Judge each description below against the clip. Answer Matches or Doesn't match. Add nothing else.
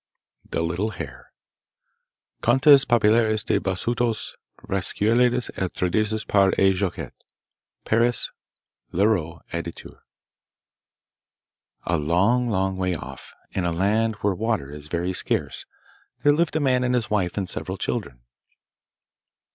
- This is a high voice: Doesn't match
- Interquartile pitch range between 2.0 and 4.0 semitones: Doesn't match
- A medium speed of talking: Doesn't match